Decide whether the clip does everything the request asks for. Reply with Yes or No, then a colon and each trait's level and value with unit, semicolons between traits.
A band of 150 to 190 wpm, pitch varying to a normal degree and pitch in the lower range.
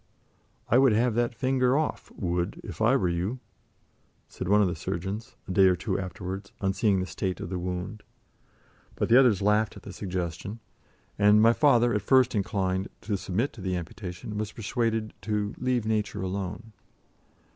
Yes: average, 180 wpm; average, 3.6 semitones; low, 105 Hz